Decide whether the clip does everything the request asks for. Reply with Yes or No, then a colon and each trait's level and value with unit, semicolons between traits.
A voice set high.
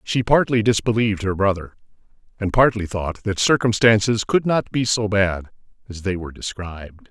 No: low, 105 Hz